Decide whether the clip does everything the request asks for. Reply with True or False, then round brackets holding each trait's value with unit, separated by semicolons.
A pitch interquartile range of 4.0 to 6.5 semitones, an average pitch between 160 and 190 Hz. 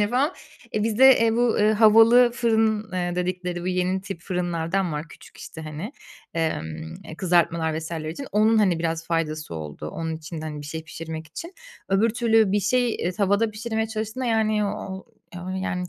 True (5.1 semitones; 185 Hz)